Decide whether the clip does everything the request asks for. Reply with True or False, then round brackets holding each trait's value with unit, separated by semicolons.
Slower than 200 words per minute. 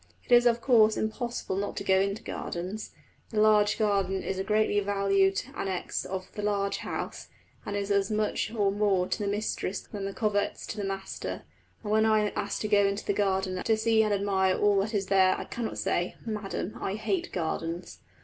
False (205 wpm)